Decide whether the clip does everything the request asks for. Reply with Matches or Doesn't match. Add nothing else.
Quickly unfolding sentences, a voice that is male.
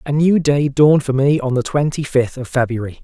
Matches